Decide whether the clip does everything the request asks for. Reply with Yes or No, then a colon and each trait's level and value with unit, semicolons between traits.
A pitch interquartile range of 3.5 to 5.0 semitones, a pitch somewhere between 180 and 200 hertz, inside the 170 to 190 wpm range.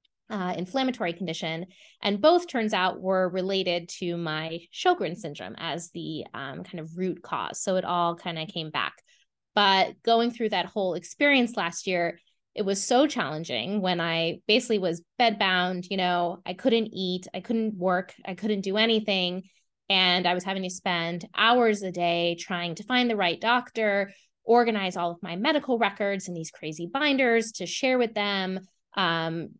Yes: average, 4.1 semitones; medium, 185 Hz; average, 175 wpm